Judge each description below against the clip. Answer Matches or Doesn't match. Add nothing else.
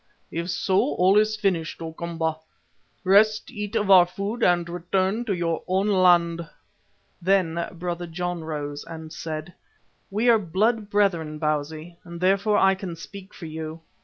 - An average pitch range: Matches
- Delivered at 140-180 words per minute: Matches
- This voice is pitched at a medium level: Matches